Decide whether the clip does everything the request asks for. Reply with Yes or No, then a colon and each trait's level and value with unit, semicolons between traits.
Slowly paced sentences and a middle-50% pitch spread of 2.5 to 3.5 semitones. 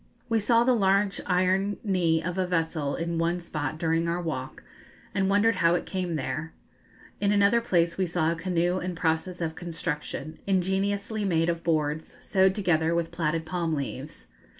No: average, 175 wpm; average, 2.9 semitones